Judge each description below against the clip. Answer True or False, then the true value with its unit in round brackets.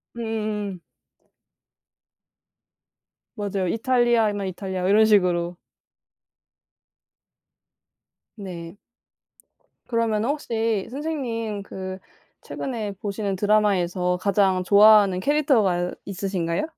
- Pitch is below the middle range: False (205 Hz)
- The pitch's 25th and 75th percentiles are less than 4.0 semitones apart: True (3.1 semitones)